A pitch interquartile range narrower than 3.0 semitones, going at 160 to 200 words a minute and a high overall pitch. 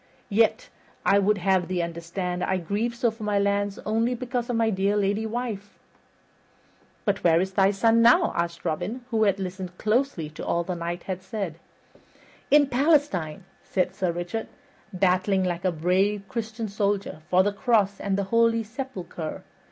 No: average, 3.8 semitones; average, 165 wpm; high, 200 Hz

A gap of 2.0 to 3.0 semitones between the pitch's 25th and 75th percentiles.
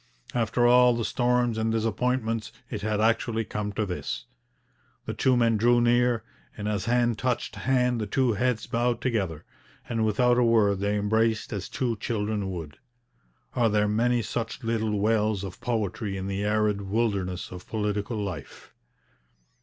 Yes: narrow, 2.6 semitones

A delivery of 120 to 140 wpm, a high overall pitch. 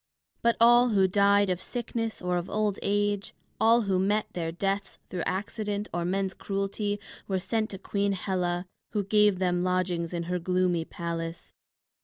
No: average, 165 wpm; high, 195 Hz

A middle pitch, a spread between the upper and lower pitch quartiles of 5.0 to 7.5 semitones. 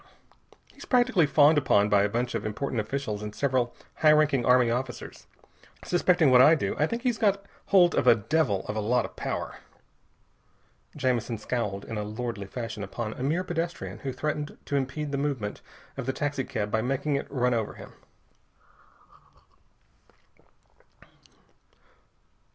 No: low, 130 Hz; average, 5.3 semitones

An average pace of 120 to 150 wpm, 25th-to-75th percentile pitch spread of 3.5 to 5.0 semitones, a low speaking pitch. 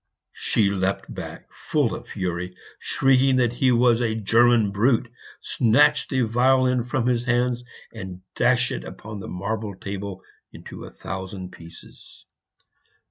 Yes: slow, 135 wpm; average, 4.1 semitones; low, 115 Hz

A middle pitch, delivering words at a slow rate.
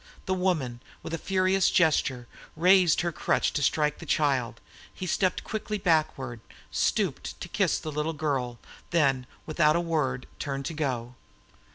No: medium, 155 Hz; average, 155 wpm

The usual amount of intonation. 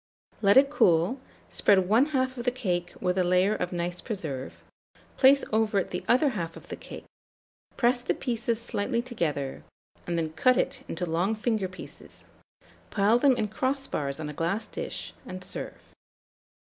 No: wide, 5.7 semitones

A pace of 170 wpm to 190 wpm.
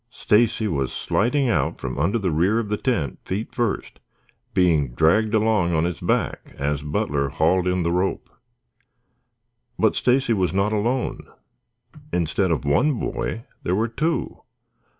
No: average, 150 wpm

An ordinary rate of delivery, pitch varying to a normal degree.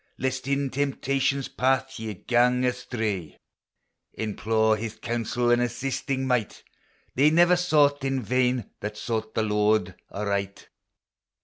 No: slow, 120 wpm; average, 3.4 semitones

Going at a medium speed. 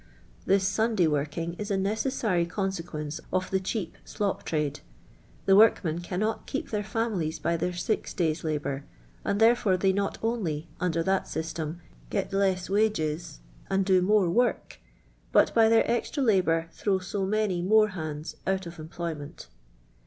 Yes: average, 170 wpm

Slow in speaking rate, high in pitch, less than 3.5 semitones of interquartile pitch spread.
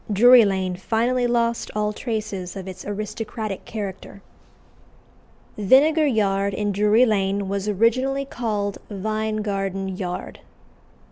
Yes: slow, 115 wpm; high, 210 Hz; average, 2.9 semitones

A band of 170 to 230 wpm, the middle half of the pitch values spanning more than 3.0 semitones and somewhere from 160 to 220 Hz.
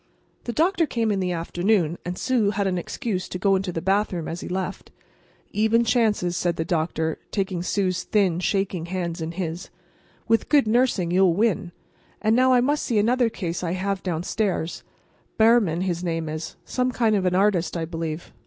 Yes: average, 180 wpm; average, 4.2 semitones; high, 190 Hz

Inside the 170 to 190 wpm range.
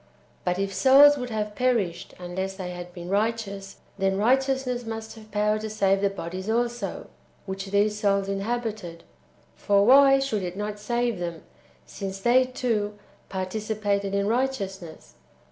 No: average, 145 wpm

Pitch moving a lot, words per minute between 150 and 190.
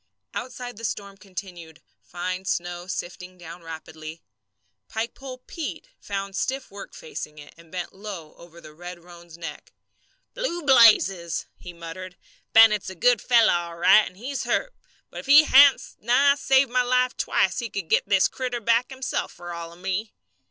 Yes: wide, 6.2 semitones; average, 165 wpm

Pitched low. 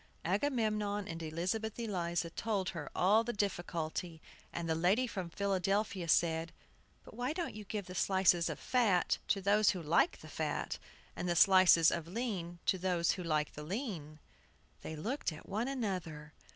No: medium, 185 Hz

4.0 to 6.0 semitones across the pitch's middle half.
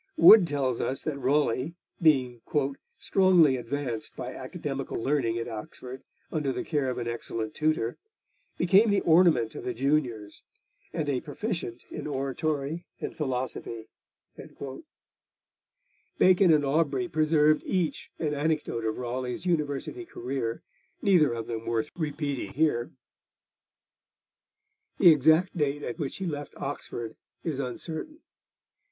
Yes: average, 4.4 semitones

